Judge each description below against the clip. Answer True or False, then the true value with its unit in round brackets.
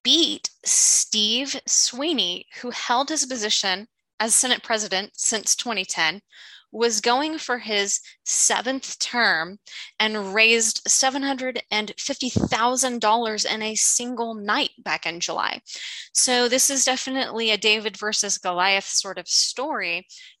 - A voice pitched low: False (225 Hz)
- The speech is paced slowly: True (115 wpm)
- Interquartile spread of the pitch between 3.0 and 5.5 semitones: True (3.7 semitones)